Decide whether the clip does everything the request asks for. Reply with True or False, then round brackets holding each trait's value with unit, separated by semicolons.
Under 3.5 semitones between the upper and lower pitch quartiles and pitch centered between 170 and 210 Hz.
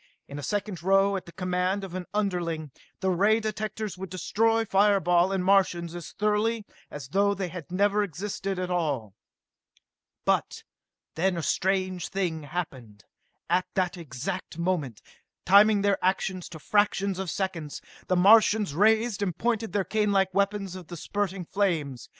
True (2.7 semitones; 190 Hz)